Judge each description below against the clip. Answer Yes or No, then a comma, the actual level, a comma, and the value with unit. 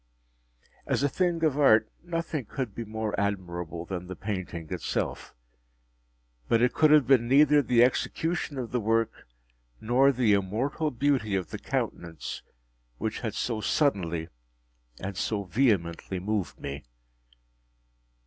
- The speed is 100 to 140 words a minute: Yes, slow, 135 wpm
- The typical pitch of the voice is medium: No, low, 110 Hz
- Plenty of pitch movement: Yes, wide, 6.4 semitones